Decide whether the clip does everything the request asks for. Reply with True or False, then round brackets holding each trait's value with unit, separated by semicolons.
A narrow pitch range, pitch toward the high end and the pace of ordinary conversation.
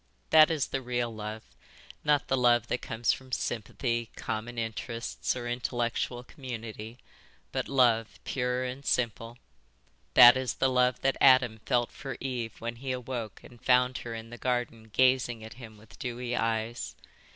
False (1.9 semitones; 120 Hz; 160 wpm)